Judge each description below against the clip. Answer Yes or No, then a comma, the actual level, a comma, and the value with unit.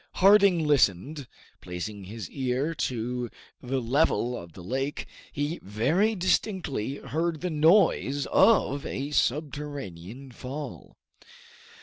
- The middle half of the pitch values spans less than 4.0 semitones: No, average, 4.9 semitones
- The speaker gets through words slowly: Yes, slow, 105 wpm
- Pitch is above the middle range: No, medium, 140 Hz